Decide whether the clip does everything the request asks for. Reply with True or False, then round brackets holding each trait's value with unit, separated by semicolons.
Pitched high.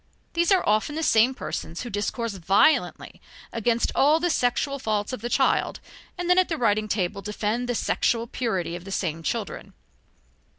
True (230 Hz)